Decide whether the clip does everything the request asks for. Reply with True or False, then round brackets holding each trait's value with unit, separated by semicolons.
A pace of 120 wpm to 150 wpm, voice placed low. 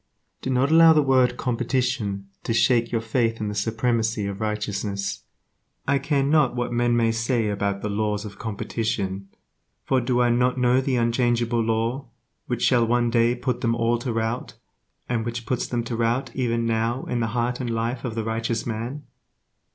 False (185 wpm; 115 Hz)